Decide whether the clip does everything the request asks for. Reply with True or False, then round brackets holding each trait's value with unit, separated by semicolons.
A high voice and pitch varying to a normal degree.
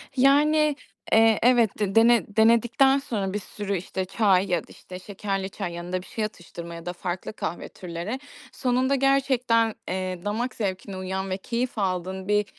True (205 Hz; 4.2 semitones)